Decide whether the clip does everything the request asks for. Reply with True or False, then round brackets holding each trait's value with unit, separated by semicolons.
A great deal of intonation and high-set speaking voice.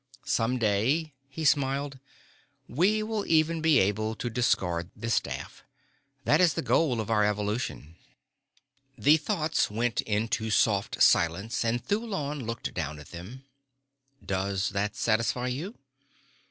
False (6.3 semitones; 115 Hz)